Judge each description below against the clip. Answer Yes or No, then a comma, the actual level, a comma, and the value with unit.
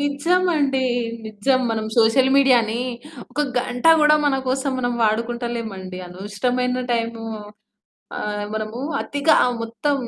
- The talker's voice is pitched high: Yes, high, 245 Hz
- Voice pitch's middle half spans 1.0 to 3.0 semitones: No, average, 3.9 semitones